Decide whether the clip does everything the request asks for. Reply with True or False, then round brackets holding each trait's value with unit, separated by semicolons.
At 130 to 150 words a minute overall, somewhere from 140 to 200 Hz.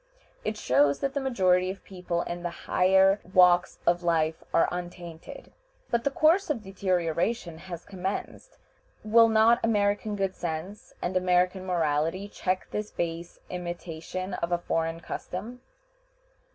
True (140 wpm; 185 Hz)